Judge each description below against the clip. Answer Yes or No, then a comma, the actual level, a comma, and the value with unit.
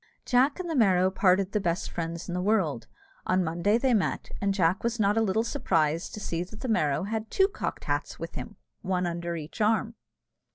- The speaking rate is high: Yes, fast, 210 wpm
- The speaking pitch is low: No, high, 195 Hz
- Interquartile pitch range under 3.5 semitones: No, average, 4.5 semitones